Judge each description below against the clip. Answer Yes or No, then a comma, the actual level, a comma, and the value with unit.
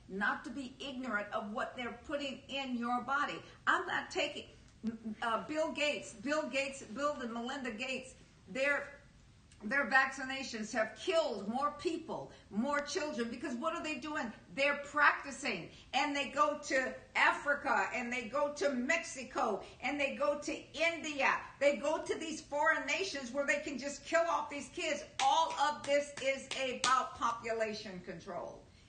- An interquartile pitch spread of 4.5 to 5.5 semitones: No, average, 3.1 semitones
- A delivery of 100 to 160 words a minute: Yes, average, 155 wpm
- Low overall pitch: No, very high, 280 Hz